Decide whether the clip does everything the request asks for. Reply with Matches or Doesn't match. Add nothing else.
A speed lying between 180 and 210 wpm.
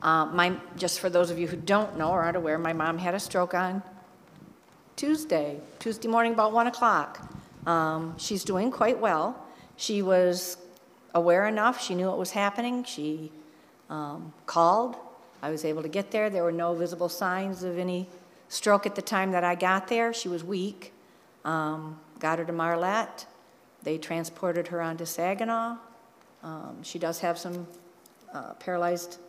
Doesn't match